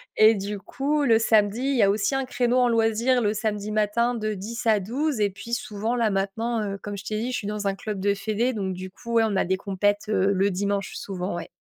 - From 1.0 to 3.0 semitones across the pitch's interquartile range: Yes, average, 2.7 semitones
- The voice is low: No, high, 215 Hz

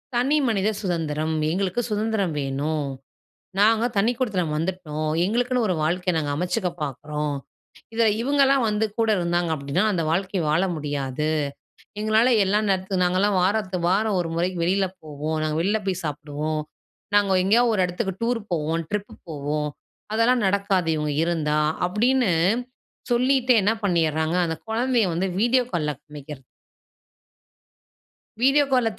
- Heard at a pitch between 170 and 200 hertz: Yes, medium, 185 Hz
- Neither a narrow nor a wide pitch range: No, wide, 5.9 semitones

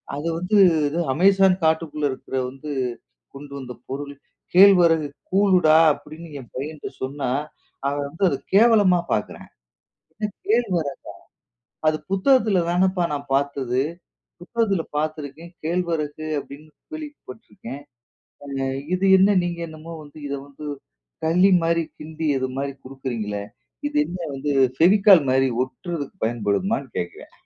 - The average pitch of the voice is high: No, medium, 160 Hz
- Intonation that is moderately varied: Yes, average, 4.8 semitones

